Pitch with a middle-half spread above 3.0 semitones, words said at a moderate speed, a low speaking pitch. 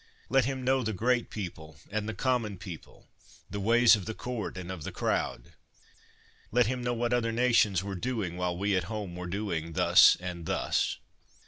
Yes: average, 5.0 semitones; average, 190 wpm; low, 105 Hz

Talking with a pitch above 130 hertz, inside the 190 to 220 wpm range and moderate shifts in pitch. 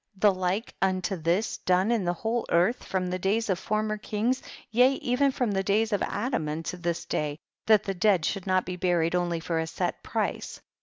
Yes: high, 190 Hz; fast, 205 wpm; average, 3.5 semitones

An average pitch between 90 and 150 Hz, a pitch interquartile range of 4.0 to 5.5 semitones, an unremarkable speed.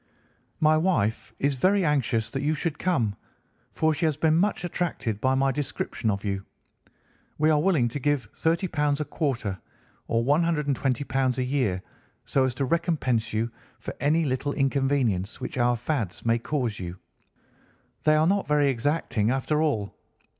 Yes: low, 135 Hz; average, 4.7 semitones; average, 165 wpm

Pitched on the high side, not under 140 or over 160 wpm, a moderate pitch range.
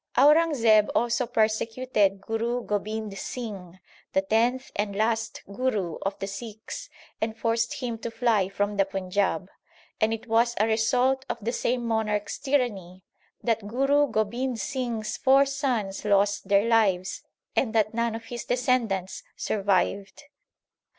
Yes: high, 225 Hz; average, 145 wpm; average, 3.1 semitones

